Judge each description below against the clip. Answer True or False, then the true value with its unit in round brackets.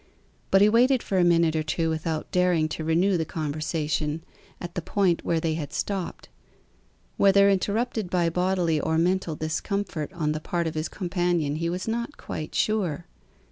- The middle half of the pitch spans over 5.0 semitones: False (3.3 semitones)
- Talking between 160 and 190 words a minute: True (175 wpm)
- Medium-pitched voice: True (170 Hz)